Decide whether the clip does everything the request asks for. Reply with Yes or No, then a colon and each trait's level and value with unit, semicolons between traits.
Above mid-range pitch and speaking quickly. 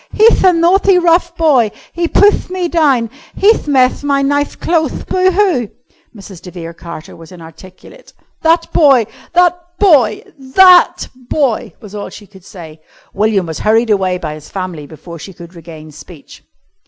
No: high, 230 Hz; average, 160 wpm